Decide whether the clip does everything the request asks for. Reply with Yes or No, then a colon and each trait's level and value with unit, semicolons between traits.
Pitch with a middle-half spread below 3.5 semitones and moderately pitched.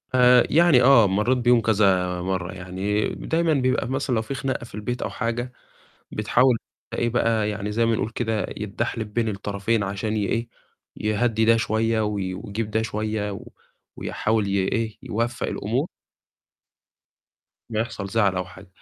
No: average, 2.7 semitones; low, 110 Hz